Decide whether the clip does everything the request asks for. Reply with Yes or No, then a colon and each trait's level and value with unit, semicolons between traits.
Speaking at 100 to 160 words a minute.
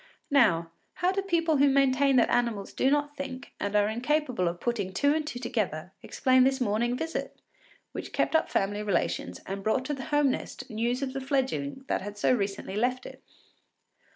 No: average, 190 wpm